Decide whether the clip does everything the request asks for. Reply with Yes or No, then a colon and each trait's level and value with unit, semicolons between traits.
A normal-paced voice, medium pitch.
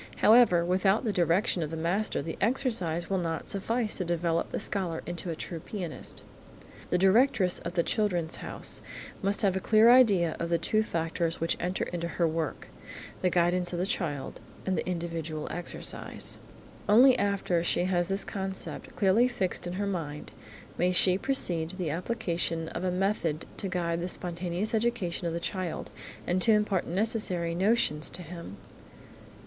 Yes: average, 170 wpm; medium, 180 Hz